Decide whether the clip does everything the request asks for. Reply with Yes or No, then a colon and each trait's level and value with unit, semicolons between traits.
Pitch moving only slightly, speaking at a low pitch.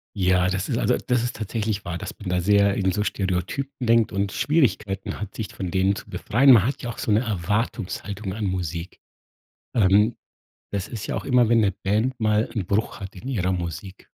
No: average, 3.1 semitones; low, 100 Hz